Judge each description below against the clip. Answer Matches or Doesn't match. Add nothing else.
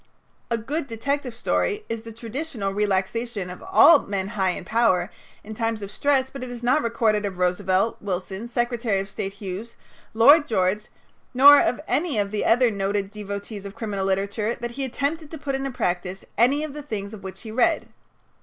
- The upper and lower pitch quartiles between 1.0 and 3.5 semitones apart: Doesn't match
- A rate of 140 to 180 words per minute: Doesn't match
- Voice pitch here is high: Matches